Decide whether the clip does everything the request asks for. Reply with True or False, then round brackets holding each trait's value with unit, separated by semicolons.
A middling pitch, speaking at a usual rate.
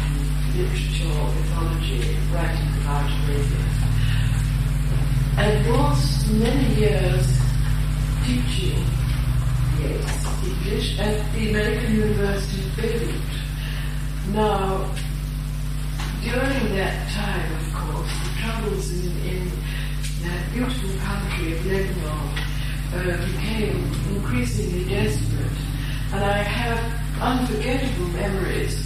False (145 Hz; 85 wpm)